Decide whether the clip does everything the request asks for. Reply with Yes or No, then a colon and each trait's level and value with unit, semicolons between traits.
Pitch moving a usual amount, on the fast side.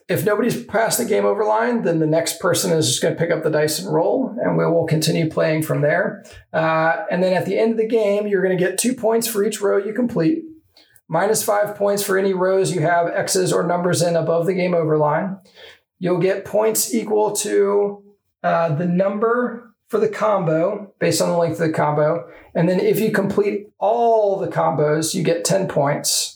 Yes: average, 4.0 semitones; fast, 215 wpm